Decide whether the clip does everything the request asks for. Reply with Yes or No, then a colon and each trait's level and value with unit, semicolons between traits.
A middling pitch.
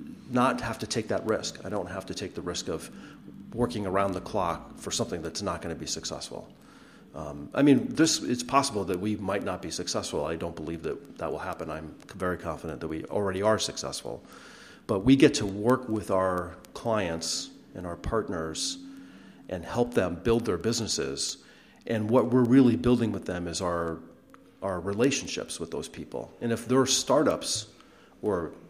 No: low, 100 Hz